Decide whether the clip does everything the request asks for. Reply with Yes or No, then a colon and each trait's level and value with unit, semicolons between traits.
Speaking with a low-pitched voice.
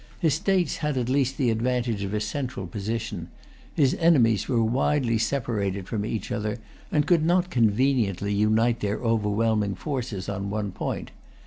Yes: low, 115 Hz